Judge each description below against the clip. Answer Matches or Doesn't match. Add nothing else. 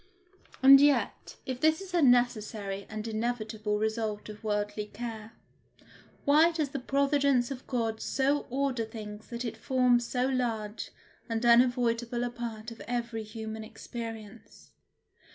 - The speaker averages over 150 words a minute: Doesn't match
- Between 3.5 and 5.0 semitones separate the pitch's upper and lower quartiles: Doesn't match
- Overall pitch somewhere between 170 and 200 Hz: Doesn't match